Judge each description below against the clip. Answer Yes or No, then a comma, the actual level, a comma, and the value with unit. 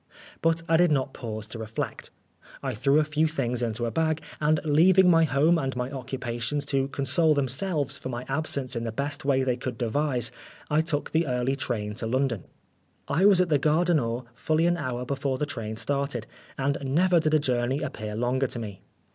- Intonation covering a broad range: No, average, 4.2 semitones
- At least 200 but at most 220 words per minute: Yes, fast, 205 wpm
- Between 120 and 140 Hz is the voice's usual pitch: Yes, low, 135 Hz